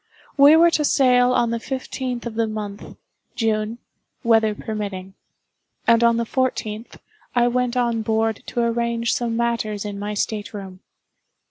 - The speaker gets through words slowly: No, average, 150 wpm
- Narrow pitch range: Yes, narrow, 2.2 semitones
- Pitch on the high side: Yes, high, 230 Hz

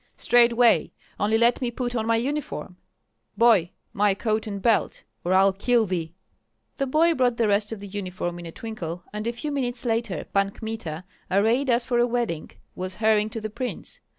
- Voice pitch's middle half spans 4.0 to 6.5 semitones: No, average, 3.4 semitones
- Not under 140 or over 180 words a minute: No, average, 190 wpm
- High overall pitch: Yes, high, 220 Hz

